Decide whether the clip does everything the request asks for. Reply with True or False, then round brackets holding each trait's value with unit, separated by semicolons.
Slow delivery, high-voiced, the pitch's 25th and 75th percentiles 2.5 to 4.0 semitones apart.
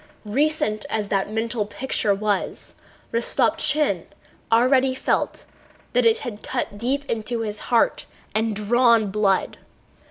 True (120 wpm; 225 Hz; 3.4 semitones)